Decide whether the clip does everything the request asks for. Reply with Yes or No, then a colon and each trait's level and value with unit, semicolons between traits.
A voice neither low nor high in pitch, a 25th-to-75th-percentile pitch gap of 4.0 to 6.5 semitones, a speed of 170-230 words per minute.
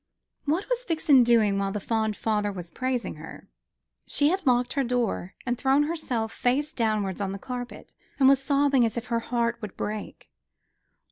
No: high, 245 Hz; average, 4.3 semitones; average, 180 wpm